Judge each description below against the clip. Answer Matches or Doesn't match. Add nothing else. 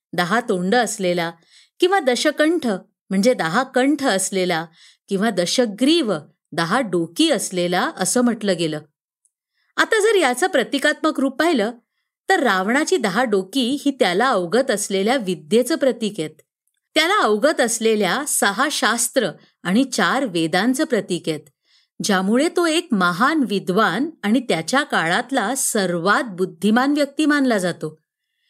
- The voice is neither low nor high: Doesn't match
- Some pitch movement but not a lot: Doesn't match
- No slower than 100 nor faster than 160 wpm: Matches